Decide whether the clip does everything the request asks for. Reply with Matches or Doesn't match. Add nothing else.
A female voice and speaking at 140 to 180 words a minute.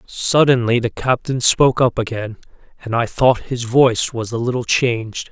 Doesn't match